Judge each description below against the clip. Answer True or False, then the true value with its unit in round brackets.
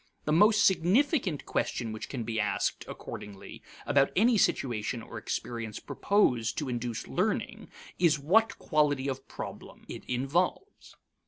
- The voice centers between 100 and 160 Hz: True (140 Hz)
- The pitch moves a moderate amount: False (7.9 semitones)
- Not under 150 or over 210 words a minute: False (135 wpm)